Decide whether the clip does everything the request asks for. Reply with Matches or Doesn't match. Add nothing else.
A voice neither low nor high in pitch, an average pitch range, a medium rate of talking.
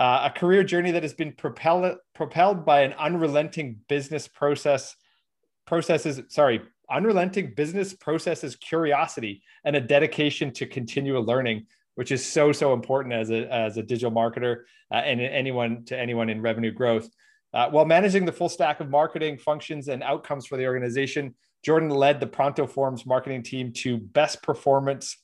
Matches